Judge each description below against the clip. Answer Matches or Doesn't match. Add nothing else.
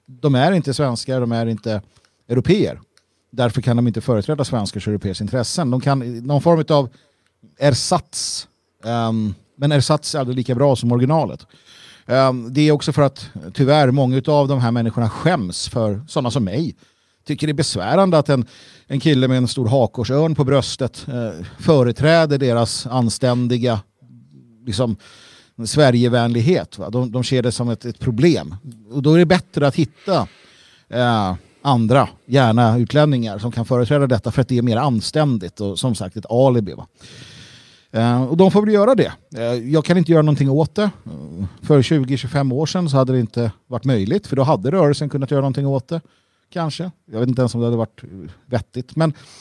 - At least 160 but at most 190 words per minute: Matches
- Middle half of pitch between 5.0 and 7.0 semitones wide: Doesn't match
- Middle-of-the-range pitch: Doesn't match